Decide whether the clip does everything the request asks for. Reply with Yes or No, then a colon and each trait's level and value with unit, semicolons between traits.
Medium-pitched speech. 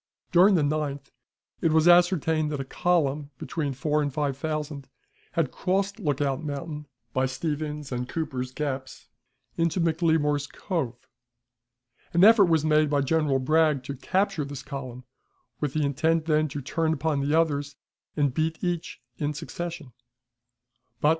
Yes: medium, 150 Hz